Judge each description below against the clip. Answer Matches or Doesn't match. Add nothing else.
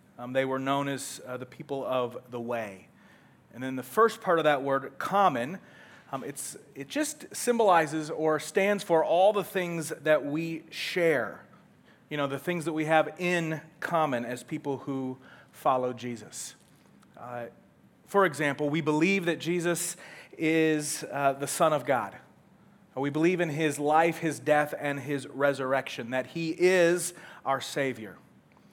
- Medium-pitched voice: Matches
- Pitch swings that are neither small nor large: Matches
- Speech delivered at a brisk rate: Doesn't match